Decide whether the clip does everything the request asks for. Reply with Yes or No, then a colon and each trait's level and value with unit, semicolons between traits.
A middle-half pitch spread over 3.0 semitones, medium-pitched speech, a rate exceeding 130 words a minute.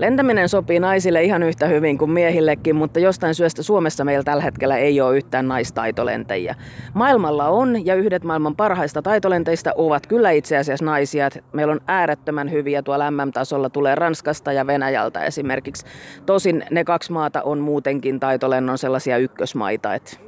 Yes: average, 3.5 semitones; medium, 150 Hz; average, 150 wpm